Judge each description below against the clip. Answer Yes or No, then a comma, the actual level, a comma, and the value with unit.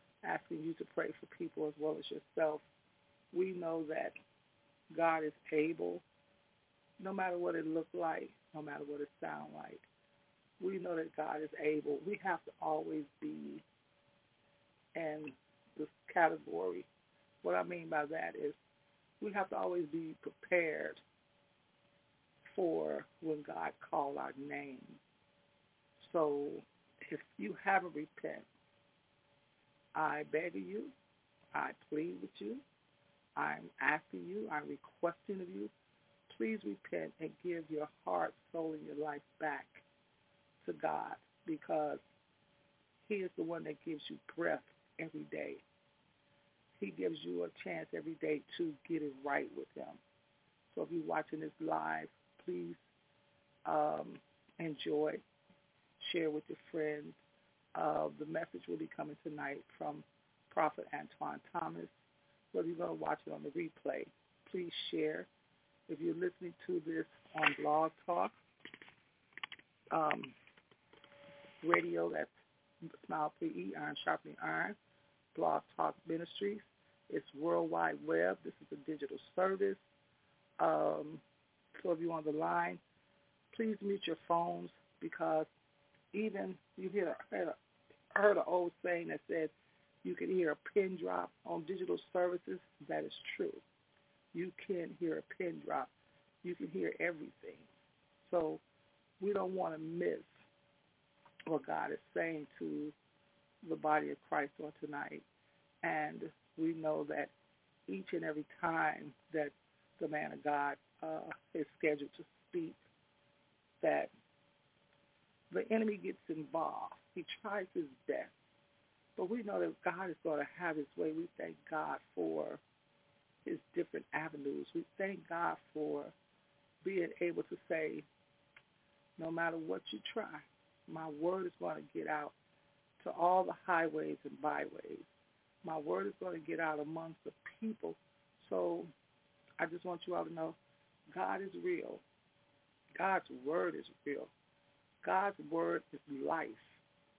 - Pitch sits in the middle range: Yes, medium, 160 Hz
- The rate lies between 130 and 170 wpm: Yes, average, 140 wpm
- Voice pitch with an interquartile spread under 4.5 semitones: Yes, average, 4.0 semitones